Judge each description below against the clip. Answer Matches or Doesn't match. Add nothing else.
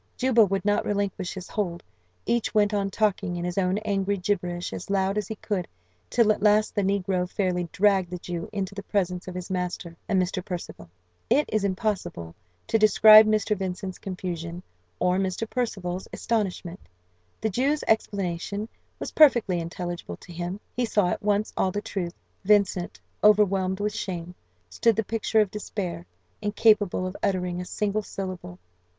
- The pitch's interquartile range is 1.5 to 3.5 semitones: Matches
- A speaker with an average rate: Matches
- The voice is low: Doesn't match